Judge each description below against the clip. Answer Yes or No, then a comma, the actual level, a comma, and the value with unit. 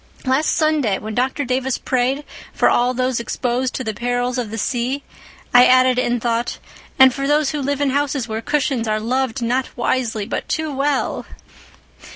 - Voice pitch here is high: Yes, very high, 255 Hz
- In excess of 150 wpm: Yes, average, 185 wpm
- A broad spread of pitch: No, narrow, 2.4 semitones